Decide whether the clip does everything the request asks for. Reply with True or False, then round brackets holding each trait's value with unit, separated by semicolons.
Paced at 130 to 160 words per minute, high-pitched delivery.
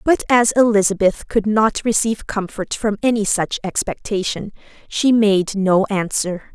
True (140 wpm; 210 Hz)